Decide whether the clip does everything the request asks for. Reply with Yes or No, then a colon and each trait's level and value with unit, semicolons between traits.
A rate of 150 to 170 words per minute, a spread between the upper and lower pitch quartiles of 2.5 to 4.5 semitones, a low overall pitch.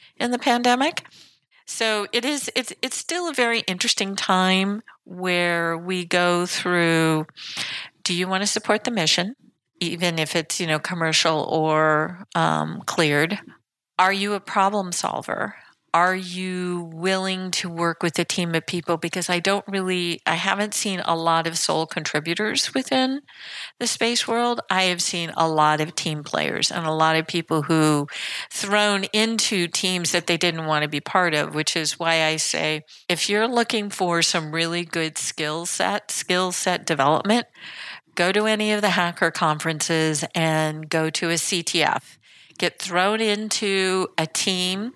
No: average, 165 wpm; average, 3.8 semitones; medium, 180 Hz